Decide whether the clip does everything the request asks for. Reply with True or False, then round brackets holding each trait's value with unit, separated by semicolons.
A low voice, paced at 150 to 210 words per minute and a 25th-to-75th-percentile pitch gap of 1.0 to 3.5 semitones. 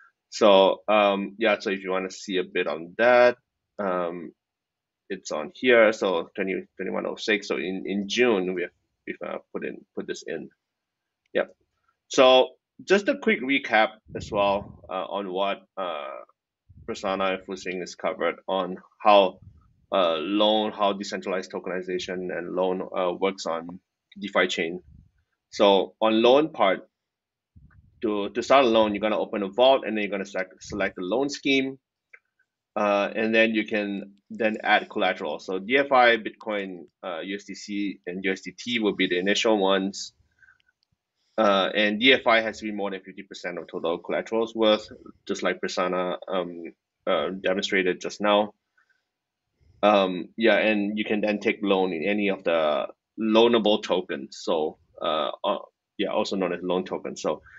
True (100 Hz; 160 wpm; 2.7 semitones)